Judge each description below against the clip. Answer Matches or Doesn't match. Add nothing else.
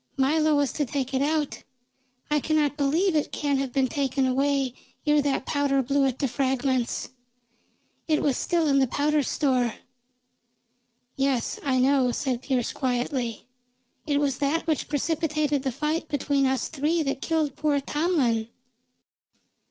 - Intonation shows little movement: Matches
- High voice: Matches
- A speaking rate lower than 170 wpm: Matches